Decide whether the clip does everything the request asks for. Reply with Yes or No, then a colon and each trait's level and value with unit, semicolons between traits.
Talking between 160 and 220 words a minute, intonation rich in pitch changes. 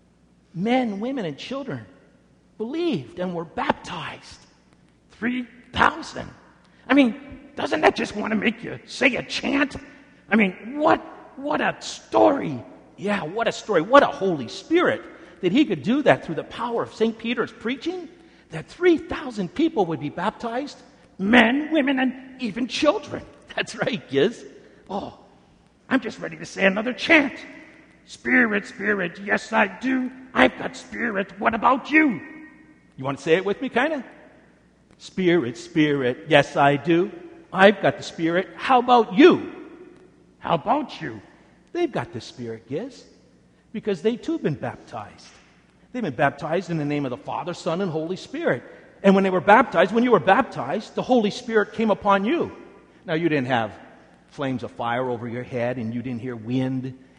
Yes: average, 165 wpm; wide, 8.8 semitones